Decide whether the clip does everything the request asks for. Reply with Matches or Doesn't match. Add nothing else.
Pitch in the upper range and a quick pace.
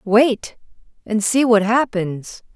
Doesn't match